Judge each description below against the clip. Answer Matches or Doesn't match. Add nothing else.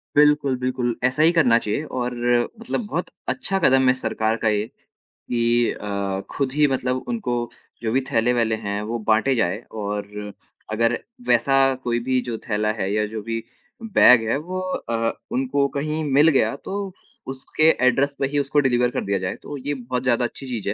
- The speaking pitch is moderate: Doesn't match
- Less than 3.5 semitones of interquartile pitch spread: Doesn't match